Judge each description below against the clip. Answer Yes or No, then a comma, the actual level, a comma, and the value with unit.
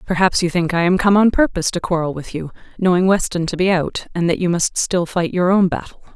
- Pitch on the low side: No, medium, 175 Hz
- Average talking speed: No, fast, 255 wpm